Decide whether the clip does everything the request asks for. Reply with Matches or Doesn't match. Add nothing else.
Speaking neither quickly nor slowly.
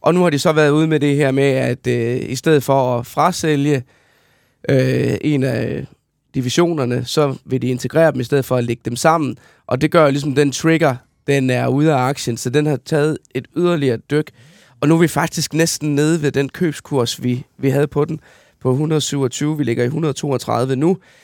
Matches